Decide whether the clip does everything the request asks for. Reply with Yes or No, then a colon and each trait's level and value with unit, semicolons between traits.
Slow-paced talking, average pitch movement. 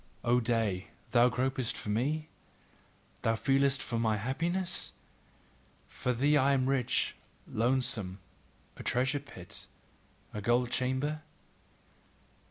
Yes: slow, 110 wpm; average, 3.2 semitones